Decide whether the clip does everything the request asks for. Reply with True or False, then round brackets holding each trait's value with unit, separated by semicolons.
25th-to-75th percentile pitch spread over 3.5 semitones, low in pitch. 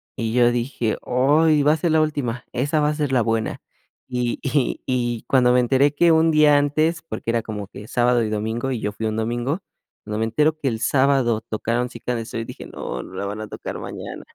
True (4.2 semitones; 125 Hz)